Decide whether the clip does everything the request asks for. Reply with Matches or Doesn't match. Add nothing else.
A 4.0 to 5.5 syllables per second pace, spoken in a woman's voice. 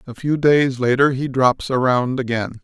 Doesn't match